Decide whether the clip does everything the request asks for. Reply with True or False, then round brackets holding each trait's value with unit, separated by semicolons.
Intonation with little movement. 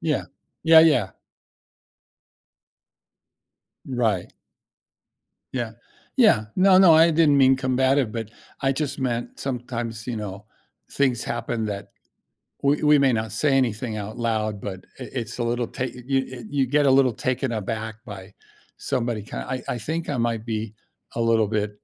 False (3.7 semitones)